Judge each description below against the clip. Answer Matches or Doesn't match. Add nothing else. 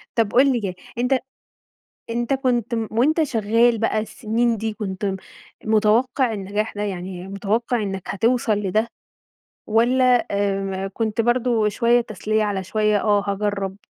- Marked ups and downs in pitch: Doesn't match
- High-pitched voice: Matches